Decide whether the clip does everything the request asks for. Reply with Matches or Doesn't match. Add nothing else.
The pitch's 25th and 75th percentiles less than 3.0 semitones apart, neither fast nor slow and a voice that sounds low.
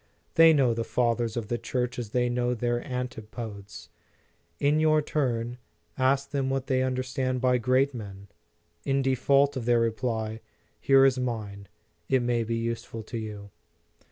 Matches